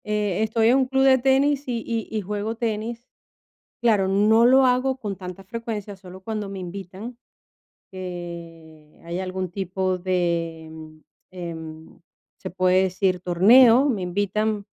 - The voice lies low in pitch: No, high, 195 Hz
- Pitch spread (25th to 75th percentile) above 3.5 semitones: Yes, average, 4.1 semitones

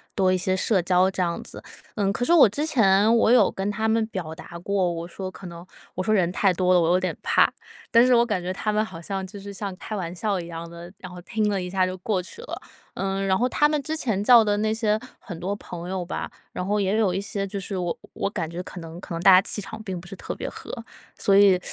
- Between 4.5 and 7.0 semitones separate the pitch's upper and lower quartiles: No, average, 2.9 semitones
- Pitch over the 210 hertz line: No, high, 195 Hz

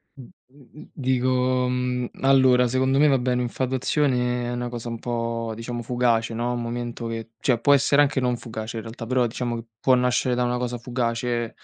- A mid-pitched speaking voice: No, low, 125 Hz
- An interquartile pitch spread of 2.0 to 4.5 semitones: No, narrow, 1.4 semitones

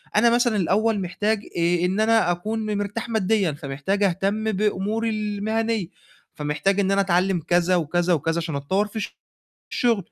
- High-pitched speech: Yes, high, 195 Hz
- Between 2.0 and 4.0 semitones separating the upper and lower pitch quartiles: Yes, average, 3.6 semitones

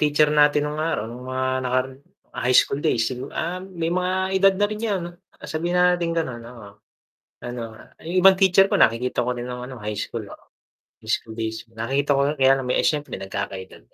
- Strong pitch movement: Yes, wide, 6.0 semitones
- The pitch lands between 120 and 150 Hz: Yes, low, 135 Hz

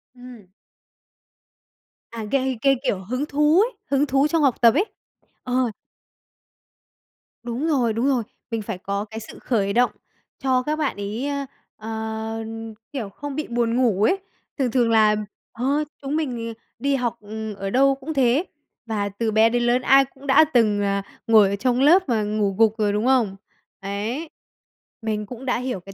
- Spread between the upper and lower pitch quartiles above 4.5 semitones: No, average, 4.0 semitones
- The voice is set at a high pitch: Yes, high, 240 Hz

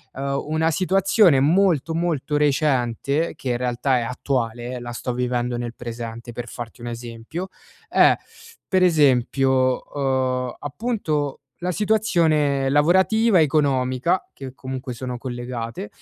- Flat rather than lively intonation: No, average, 4.6 semitones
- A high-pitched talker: No, low, 135 Hz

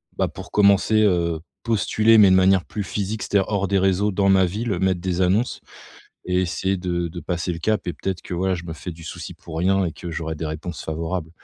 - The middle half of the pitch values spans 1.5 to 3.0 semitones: Yes, narrow, 2.4 semitones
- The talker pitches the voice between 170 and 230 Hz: No, very low, 95 Hz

